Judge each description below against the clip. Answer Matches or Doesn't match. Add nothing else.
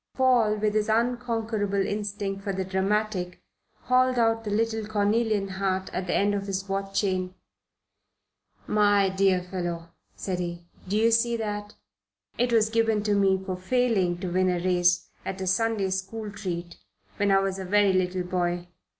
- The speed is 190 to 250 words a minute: Doesn't match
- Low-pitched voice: Doesn't match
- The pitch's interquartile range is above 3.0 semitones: Doesn't match